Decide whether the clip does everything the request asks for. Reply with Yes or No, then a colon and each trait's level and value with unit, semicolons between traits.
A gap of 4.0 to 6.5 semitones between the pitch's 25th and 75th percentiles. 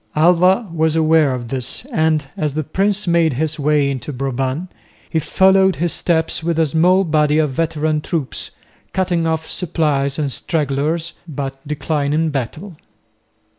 No: average, 2.9 semitones